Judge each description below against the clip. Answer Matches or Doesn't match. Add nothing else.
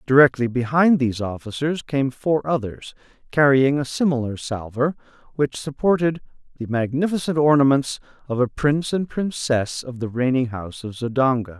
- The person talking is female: Doesn't match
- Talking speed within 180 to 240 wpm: Doesn't match